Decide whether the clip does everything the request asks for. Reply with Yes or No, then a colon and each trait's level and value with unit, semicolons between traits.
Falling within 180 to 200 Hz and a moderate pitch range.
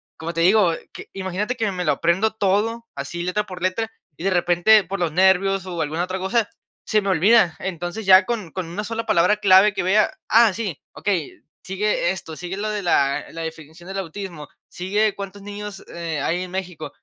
Yes: high, 190 Hz; average, 3.2 semitones